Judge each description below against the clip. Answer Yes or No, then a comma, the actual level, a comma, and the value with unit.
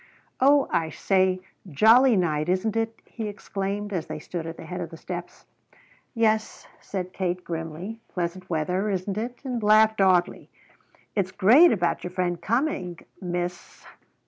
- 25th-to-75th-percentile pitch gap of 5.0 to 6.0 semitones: No, average, 3.7 semitones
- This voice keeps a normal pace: Yes, average, 150 wpm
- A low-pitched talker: No, medium, 185 Hz